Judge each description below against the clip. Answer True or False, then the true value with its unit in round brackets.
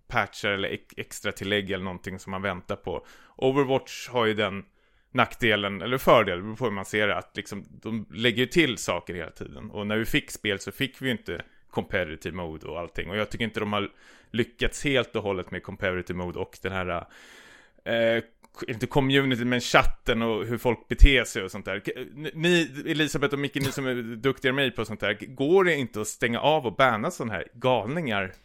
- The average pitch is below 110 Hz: False (115 Hz)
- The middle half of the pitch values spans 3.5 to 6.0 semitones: True (4.1 semitones)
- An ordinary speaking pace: False (205 wpm)